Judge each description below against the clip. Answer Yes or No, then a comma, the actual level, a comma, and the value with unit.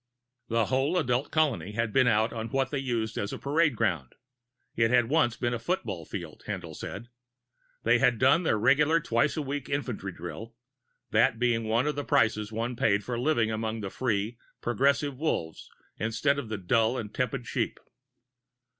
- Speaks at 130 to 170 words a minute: No, average, 180 wpm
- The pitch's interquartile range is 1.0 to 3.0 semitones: No, average, 3.8 semitones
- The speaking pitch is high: No, low, 120 Hz